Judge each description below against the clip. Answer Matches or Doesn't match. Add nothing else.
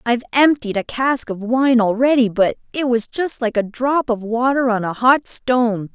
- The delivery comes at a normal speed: Doesn't match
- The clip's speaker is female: Matches